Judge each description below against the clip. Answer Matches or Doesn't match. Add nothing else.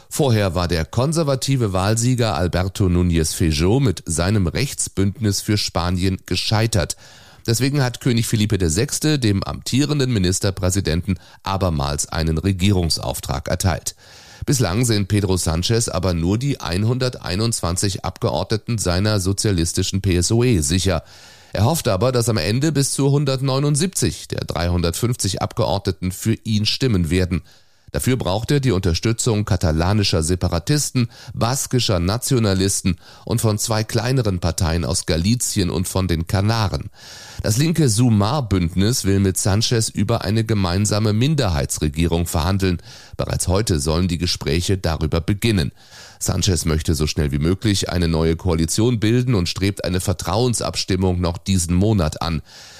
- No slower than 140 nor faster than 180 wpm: Doesn't match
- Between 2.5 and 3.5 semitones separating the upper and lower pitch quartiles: Doesn't match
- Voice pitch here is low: Matches